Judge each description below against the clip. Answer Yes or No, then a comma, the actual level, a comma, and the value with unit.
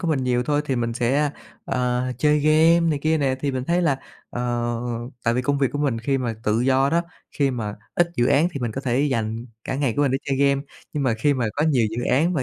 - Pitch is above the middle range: No, low, 135 Hz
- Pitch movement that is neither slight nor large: Yes, average, 3.2 semitones